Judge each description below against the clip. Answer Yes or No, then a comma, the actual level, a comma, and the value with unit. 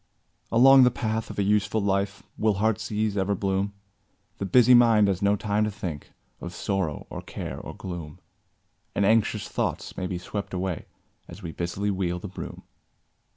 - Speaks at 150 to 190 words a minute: Yes, average, 175 wpm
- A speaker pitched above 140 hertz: No, low, 100 Hz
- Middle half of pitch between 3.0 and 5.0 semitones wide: No, narrow, 2.5 semitones